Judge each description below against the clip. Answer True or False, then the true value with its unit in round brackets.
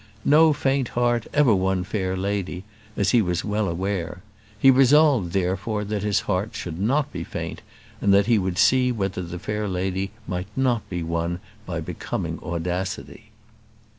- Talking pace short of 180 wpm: True (165 wpm)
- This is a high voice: False (100 Hz)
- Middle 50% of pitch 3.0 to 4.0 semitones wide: False (4.5 semitones)